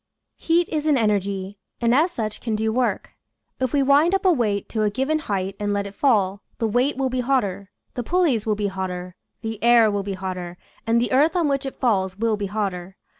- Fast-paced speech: Yes, fast, 225 wpm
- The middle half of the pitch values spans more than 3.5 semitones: Yes, average, 5.0 semitones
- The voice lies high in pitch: Yes, high, 220 Hz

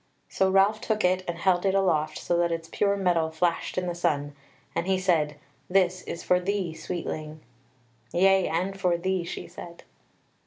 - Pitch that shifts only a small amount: Yes, narrow, 2.3 semitones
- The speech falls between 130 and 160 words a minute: No, average, 180 wpm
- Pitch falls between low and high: Yes, medium, 180 Hz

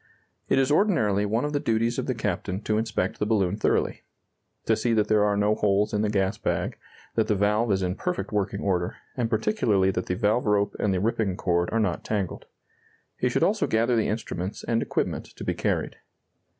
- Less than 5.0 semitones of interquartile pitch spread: Yes, narrow, 2.5 semitones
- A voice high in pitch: No, low, 105 Hz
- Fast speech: Yes, fast, 210 wpm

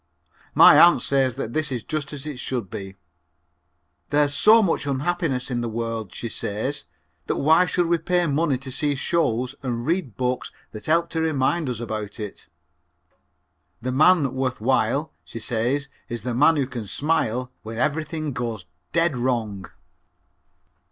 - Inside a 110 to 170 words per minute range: Yes, average, 160 wpm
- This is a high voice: No, low, 130 Hz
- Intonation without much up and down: No, average, 4.8 semitones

